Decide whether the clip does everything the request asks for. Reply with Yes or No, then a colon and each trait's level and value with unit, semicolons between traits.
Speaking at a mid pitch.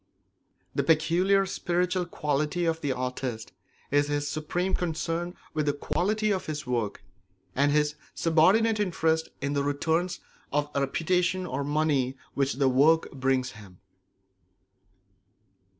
Yes: medium, 155 Hz